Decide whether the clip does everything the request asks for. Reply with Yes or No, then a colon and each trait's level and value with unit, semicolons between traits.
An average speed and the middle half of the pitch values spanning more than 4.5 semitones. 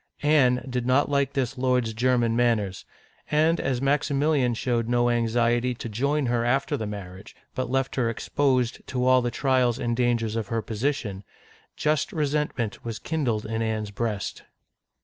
No: average, 160 wpm; average, 2.9 semitones